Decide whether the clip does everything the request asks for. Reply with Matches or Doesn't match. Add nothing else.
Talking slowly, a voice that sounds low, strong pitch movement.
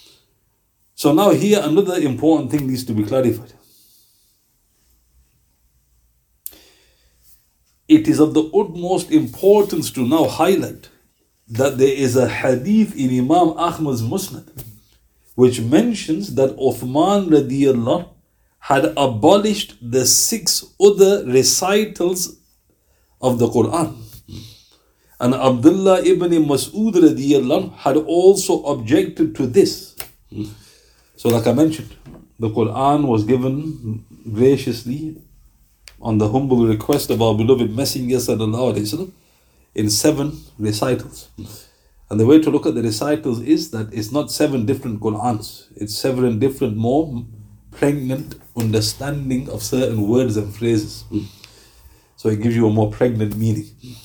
Matches